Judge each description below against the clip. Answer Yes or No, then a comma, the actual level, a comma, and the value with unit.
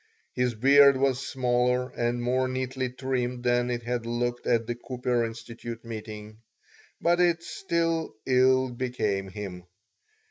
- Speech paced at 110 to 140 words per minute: Yes, slow, 135 wpm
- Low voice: Yes, low, 125 Hz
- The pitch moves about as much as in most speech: No, narrow, 1.7 semitones